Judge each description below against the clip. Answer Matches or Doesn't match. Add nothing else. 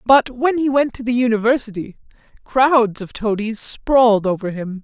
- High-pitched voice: Matches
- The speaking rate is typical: Matches